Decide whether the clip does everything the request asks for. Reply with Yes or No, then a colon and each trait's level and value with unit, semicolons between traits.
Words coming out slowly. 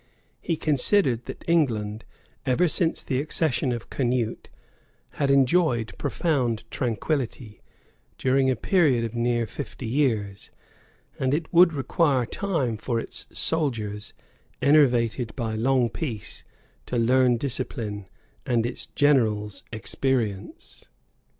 Yes: slow, 110 wpm